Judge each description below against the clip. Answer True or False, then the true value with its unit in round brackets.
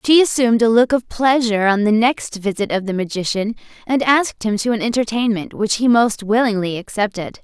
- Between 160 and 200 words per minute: True (195 wpm)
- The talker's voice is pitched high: True (225 Hz)